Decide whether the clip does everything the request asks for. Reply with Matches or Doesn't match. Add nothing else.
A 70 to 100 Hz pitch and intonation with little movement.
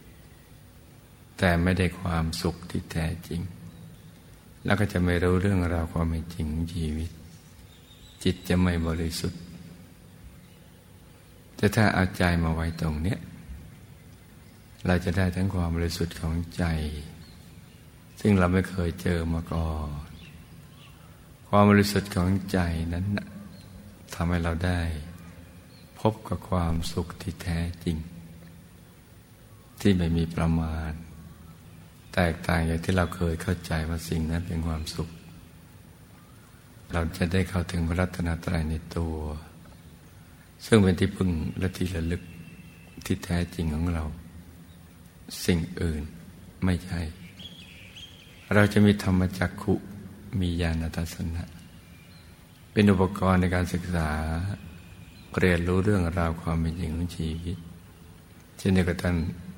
Matches